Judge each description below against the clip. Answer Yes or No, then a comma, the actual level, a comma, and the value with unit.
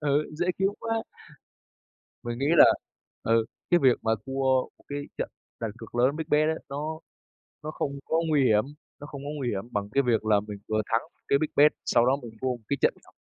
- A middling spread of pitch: Yes, average, 4.7 semitones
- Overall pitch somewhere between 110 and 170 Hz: Yes, low, 135 Hz